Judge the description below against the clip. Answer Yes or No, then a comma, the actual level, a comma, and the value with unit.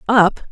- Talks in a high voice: Yes, high, 210 Hz